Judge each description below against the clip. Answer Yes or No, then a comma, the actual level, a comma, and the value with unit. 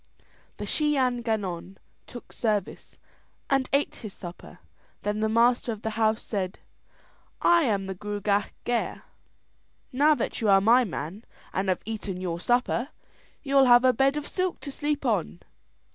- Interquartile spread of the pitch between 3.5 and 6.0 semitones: Yes, average, 4.6 semitones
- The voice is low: No, high, 225 Hz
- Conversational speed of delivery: Yes, average, 160 wpm